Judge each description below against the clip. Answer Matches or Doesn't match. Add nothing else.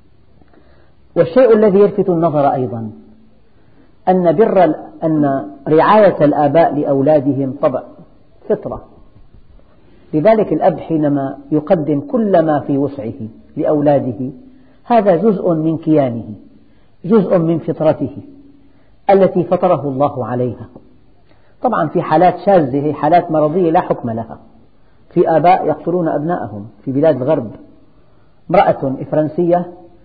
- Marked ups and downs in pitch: Doesn't match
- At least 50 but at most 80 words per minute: Doesn't match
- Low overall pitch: Doesn't match